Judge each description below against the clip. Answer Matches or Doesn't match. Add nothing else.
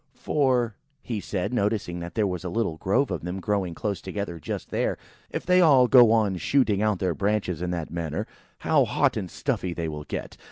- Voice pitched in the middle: Doesn't match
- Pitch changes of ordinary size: Matches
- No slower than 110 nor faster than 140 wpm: Doesn't match